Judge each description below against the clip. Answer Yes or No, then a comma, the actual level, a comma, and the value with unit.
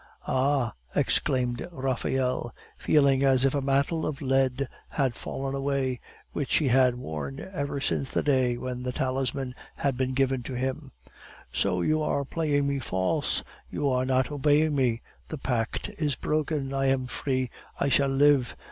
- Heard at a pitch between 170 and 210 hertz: No, low, 135 Hz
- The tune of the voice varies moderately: No, narrow, 1.8 semitones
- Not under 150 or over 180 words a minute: Yes, average, 160 wpm